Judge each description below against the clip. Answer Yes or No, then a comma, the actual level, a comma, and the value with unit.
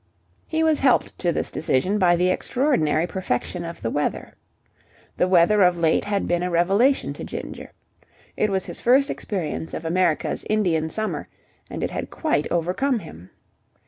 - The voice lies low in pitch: No, medium, 180 Hz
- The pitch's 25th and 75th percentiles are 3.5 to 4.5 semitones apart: Yes, average, 4.2 semitones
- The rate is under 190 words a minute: Yes, average, 165 wpm